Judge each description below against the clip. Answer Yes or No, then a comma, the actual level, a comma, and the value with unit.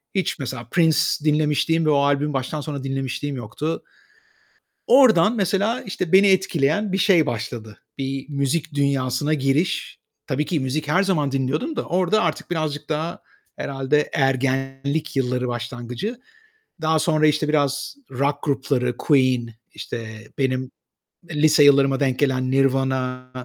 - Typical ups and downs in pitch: Yes, average, 3.2 semitones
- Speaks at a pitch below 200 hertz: Yes, medium, 140 Hz